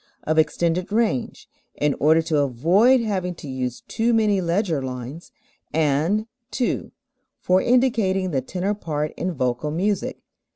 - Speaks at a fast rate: No, slow, 135 wpm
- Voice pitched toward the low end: No, medium, 170 Hz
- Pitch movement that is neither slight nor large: No, wide, 5.7 semitones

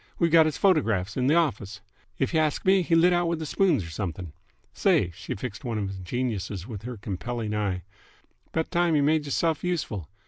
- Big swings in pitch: Yes, wide, 8.3 semitones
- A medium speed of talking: No, fast, 210 wpm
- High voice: No, low, 125 Hz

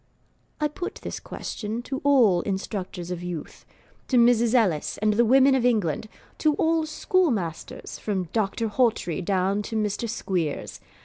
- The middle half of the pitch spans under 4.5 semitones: No, average, 5.0 semitones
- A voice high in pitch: Yes, high, 215 Hz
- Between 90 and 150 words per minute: Yes, average, 145 wpm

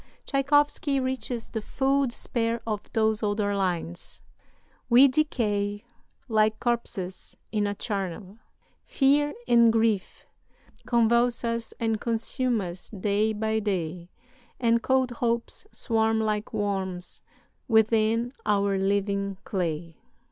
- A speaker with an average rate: No, slow, 110 wpm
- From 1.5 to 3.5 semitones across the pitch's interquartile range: Yes, average, 2.8 semitones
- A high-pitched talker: Yes, high, 220 Hz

